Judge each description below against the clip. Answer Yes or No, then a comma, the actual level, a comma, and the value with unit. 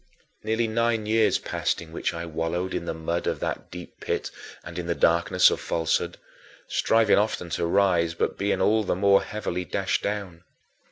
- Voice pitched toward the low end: Yes, very low, 90 Hz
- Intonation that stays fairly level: No, average, 4.0 semitones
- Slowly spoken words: No, average, 180 wpm